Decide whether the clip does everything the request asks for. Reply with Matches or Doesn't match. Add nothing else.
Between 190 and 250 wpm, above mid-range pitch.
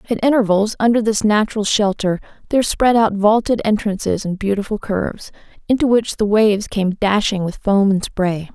Doesn't match